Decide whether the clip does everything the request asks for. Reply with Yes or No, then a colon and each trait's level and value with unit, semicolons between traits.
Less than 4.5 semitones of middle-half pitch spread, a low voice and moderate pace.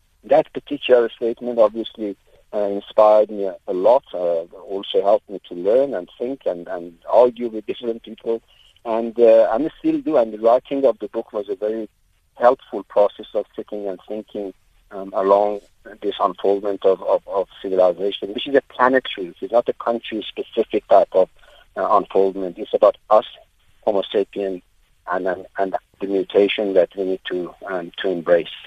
Yes: average, 2.9 semitones; low, 105 Hz; average, 165 wpm